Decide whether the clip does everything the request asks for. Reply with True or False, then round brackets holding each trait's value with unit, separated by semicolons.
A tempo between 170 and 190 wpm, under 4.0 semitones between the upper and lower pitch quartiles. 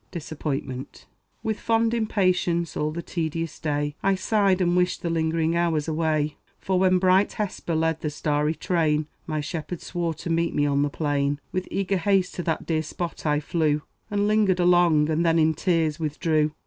True (180 wpm; 3.0 semitones)